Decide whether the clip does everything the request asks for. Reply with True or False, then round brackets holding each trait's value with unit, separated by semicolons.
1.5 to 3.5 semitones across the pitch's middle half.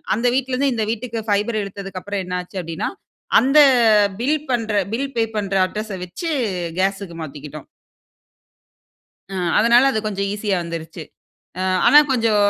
False (4.2 semitones)